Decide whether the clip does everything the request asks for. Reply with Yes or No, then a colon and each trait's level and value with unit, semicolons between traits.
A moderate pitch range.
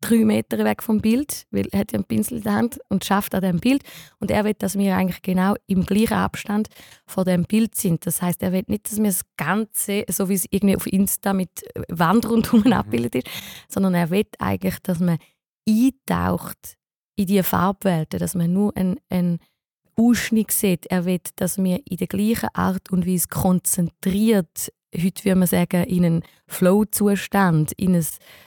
Yes: average, 3.0 semitones